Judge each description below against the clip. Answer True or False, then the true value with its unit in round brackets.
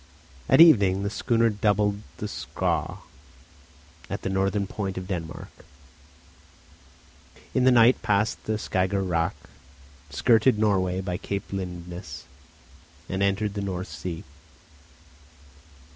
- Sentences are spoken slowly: True (115 wpm)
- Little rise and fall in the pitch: True (2.3 semitones)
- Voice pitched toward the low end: True (100 Hz)